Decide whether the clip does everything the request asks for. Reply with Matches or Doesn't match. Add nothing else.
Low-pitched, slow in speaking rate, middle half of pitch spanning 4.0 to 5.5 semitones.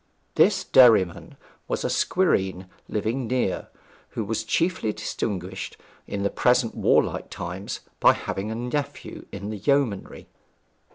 Matches